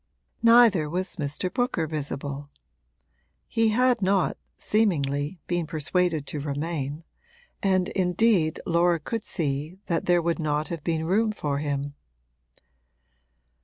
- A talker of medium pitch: Yes, medium, 170 Hz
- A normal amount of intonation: Yes, average, 4.4 semitones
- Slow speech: Yes, slow, 120 wpm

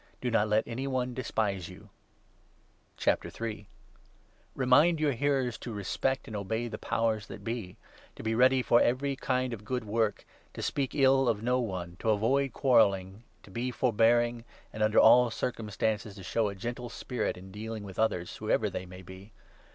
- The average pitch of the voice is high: No, low, 115 Hz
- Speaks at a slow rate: No, average, 180 wpm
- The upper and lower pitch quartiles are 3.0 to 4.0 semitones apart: Yes, average, 3.3 semitones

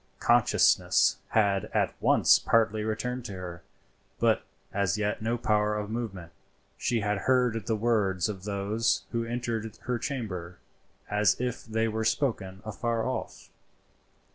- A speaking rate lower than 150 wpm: Yes, average, 140 wpm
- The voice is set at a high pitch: No, low, 110 Hz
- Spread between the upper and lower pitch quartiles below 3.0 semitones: Yes, narrow, 2.6 semitones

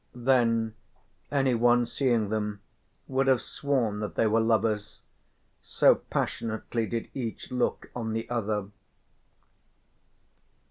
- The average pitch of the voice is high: No, low, 115 Hz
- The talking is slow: Yes, slow, 105 wpm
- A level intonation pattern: Yes, narrow, 2.0 semitones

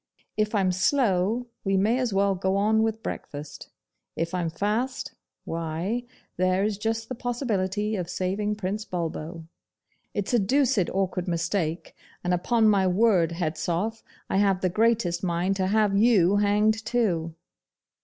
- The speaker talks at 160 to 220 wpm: No, average, 145 wpm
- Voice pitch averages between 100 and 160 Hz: No, high, 195 Hz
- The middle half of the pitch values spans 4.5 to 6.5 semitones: No, average, 3.5 semitones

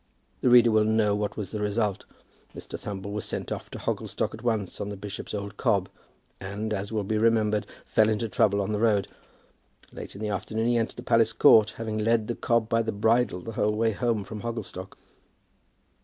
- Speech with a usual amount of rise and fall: No, narrow, 1.8 semitones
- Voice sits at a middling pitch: No, low, 110 Hz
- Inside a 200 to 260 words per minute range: Yes, fast, 205 wpm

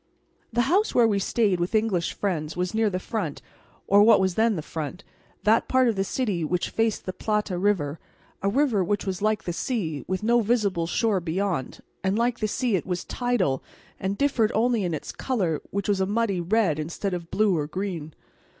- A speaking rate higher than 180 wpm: Yes, fast, 205 wpm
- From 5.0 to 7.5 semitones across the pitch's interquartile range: No, average, 4.2 semitones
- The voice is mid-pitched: No, high, 200 Hz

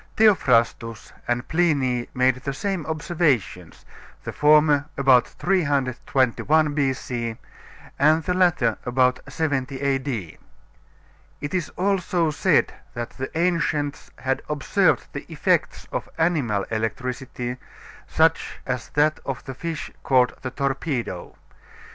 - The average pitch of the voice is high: No, medium, 140 Hz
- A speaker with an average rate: No, slow, 110 wpm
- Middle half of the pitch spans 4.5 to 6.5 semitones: No, average, 4.0 semitones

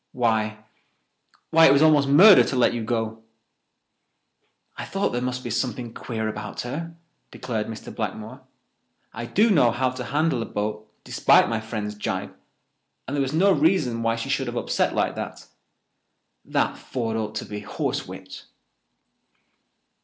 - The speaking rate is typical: Yes, average, 150 wpm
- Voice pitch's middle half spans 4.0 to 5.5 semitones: Yes, average, 4.3 semitones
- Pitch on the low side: Yes, low, 120 Hz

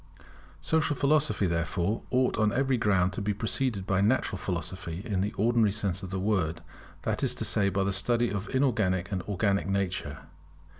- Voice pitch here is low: Yes, low, 100 Hz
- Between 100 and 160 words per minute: No, average, 180 wpm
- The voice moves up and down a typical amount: Yes, average, 3.7 semitones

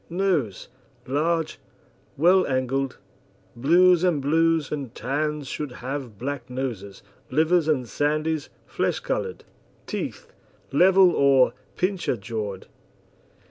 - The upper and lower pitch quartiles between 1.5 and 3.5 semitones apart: No, average, 4.3 semitones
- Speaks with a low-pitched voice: No, medium, 145 Hz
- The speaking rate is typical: No, slow, 100 wpm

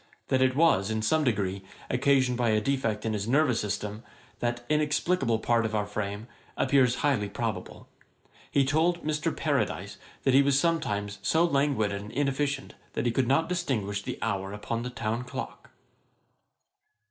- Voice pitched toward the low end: Yes, low, 125 Hz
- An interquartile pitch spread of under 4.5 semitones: No, average, 4.9 semitones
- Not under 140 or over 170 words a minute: Yes, average, 160 wpm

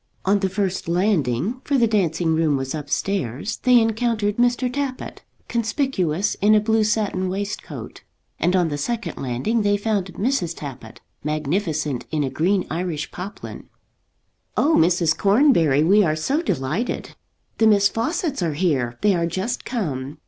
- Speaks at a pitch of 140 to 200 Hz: Yes, high, 190 Hz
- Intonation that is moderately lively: No, wide, 6.0 semitones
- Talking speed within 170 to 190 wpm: No, average, 150 wpm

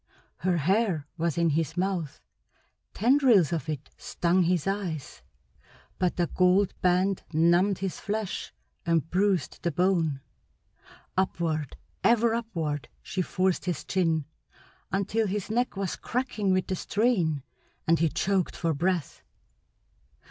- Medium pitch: Yes, medium, 180 Hz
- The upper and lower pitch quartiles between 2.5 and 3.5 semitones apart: Yes, average, 3.2 semitones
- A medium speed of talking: No, slow, 125 wpm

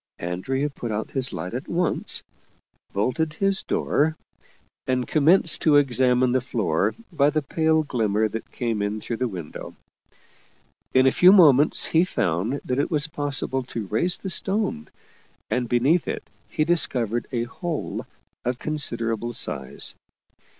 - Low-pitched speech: Yes, low, 130 Hz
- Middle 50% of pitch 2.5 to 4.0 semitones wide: No, average, 5.3 semitones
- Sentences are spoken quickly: No, average, 145 wpm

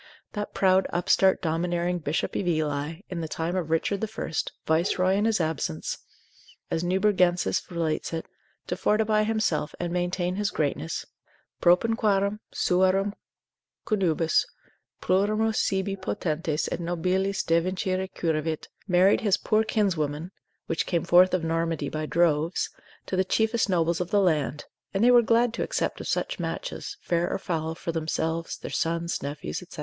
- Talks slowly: No, average, 150 wpm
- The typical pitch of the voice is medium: Yes, medium, 180 Hz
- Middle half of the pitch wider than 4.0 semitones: No, average, 3.2 semitones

